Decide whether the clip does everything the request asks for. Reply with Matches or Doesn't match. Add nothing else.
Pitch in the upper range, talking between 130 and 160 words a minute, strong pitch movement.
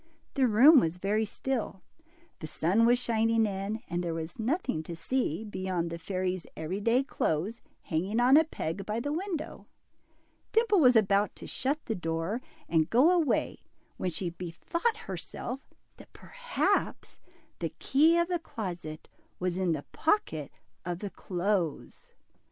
Matches